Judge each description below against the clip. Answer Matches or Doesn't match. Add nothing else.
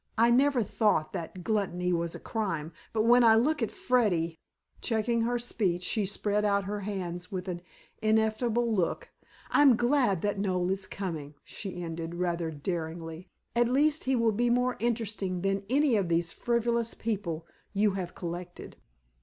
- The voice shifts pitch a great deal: Doesn't match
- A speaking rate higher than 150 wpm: Matches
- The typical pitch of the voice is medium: Doesn't match